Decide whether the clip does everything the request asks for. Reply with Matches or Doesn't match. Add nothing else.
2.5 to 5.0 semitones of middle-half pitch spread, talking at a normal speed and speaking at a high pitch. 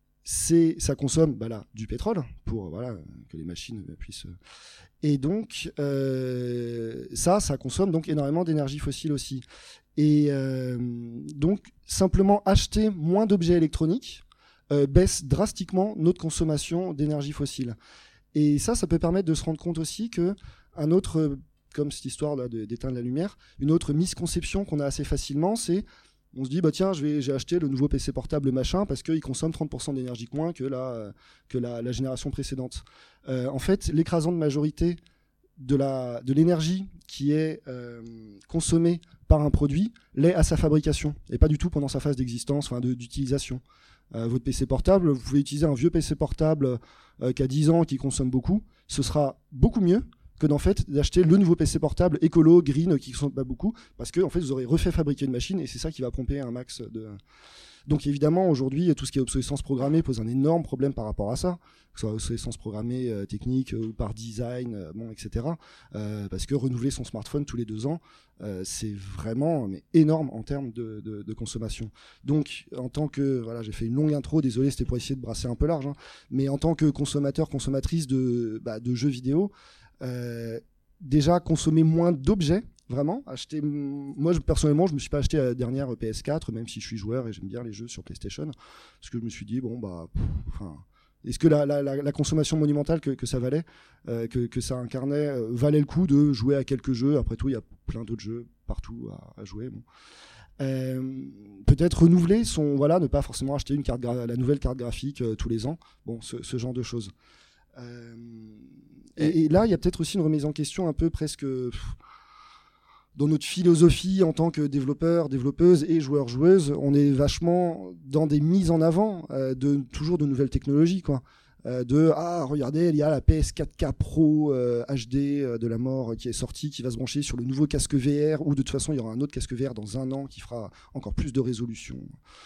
Doesn't match